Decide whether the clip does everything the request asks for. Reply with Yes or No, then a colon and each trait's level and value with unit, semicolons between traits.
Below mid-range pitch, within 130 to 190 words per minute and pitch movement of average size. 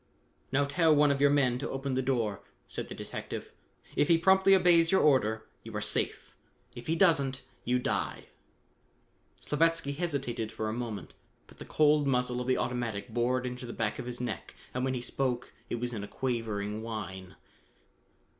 Yes: low, 125 Hz; average, 185 wpm; average, 3.6 semitones